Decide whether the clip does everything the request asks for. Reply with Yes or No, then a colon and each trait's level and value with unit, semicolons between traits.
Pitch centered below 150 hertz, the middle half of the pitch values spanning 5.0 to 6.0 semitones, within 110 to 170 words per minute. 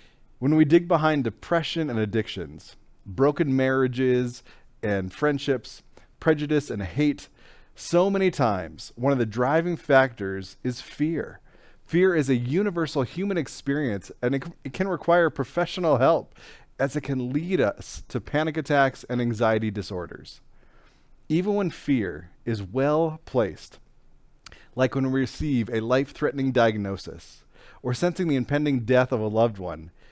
Yes: low, 135 Hz; wide, 5.4 semitones; average, 140 wpm